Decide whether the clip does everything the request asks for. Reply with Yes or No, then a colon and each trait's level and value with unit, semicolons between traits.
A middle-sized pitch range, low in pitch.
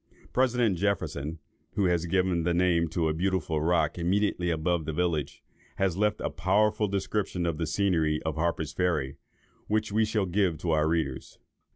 Yes: average, 3.7 semitones; very low, 90 Hz